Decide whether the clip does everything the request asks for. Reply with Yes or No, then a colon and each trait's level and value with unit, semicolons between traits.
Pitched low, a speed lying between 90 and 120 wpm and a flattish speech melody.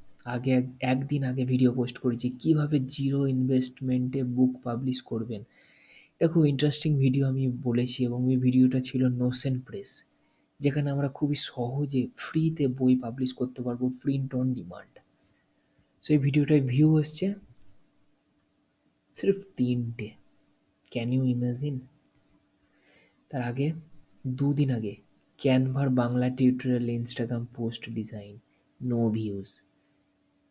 Yes: low, 130 Hz; average, 115 wpm; narrow, 2.2 semitones